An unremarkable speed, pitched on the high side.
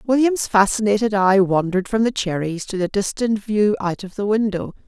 Yes: average, 185 wpm; high, 205 Hz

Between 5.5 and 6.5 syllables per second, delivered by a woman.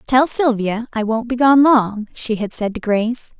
No: 4.5 syllables/s; female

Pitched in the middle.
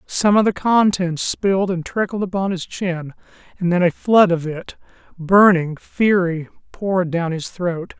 Yes: medium, 180 Hz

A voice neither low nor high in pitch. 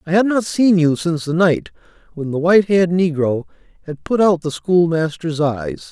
Yes: medium, 170 Hz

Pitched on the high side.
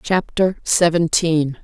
No: medium, 170 Hz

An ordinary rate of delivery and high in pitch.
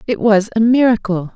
Yes: average, 175 wpm; high, 215 Hz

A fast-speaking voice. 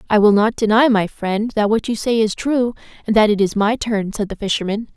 Yes: fast, 255 wpm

